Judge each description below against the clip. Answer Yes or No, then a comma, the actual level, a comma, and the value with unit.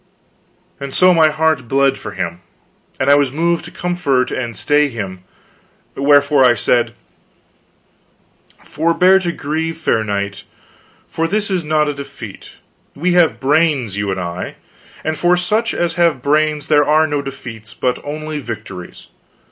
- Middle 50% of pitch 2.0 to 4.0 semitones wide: No, average, 4.4 semitones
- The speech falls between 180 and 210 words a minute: No, average, 150 wpm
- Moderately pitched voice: Yes, medium, 145 Hz